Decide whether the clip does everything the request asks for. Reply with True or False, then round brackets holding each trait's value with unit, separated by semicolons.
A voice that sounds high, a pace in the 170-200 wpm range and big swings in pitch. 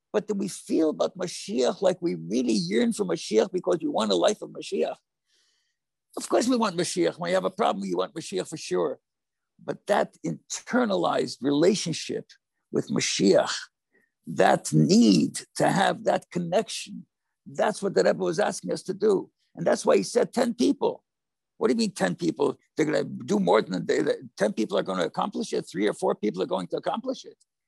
True (205 Hz; 195 wpm; 8.3 semitones)